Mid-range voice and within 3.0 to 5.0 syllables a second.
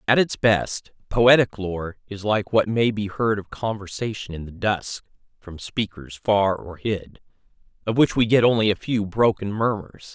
No: low, 105 Hz; 4.3 syllables/s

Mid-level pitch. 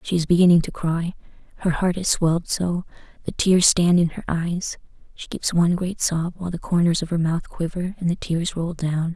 Yes: medium, 170 Hz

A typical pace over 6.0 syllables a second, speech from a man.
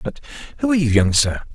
Yes: 7.1 syllables/s; male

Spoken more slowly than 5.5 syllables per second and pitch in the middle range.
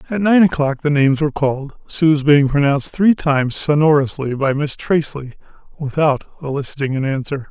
No: 5.6 syllables/s; medium, 145 Hz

